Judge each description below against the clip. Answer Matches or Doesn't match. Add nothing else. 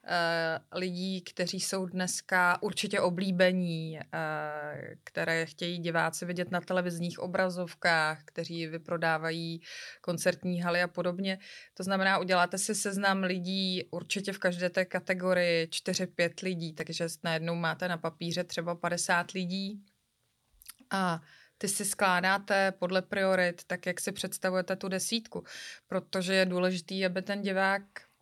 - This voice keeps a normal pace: Matches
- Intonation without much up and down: Matches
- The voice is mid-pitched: Matches